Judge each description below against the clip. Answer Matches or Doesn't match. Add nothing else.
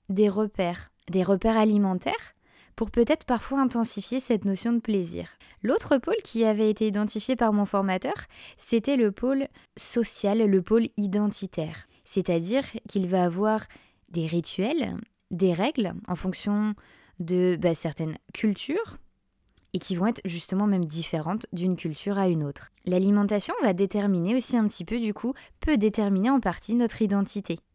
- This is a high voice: Matches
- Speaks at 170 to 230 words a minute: Doesn't match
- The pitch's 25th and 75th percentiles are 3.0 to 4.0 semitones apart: Matches